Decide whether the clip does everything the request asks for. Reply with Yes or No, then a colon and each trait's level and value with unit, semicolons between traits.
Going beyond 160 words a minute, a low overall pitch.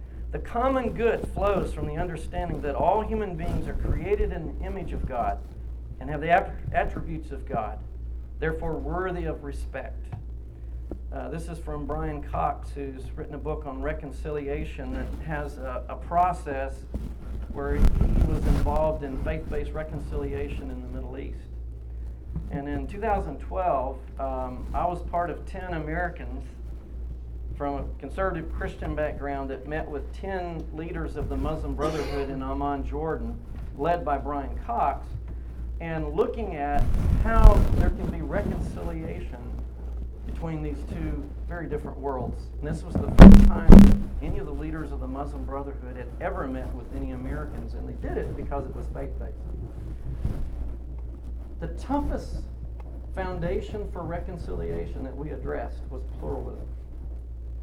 No: average, 145 wpm; very low, 65 Hz